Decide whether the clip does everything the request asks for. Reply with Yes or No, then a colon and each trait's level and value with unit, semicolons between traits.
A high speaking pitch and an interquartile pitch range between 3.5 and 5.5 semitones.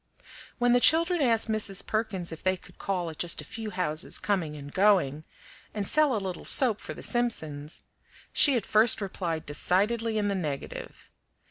Yes: high, 200 Hz; average, 5.1 semitones